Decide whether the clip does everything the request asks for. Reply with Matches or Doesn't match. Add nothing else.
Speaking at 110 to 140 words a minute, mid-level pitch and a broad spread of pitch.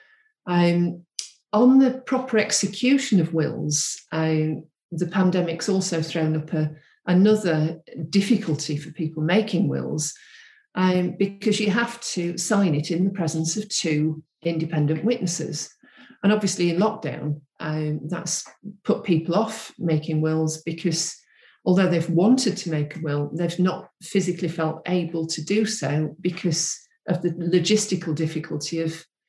Doesn't match